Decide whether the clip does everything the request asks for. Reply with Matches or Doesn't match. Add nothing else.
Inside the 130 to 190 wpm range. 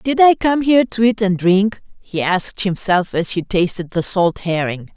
Doesn't match